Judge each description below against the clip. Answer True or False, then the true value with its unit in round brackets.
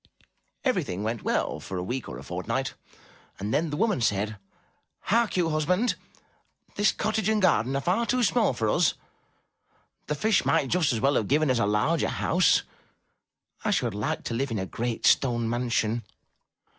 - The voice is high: False (135 Hz)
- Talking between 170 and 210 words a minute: True (175 wpm)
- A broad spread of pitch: True (8.4 semitones)